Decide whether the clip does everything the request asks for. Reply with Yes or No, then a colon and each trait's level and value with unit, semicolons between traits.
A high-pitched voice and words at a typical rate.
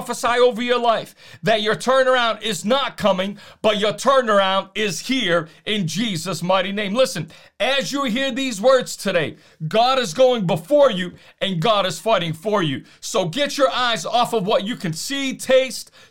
Yes: high, 220 Hz; average, 180 wpm